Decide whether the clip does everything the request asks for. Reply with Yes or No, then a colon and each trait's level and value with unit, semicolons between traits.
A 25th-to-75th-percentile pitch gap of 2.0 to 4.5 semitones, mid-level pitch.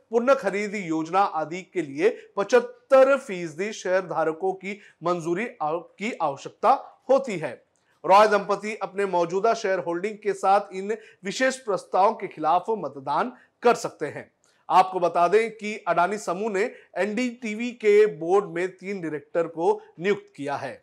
No: average, 4.0 semitones; high, 200 Hz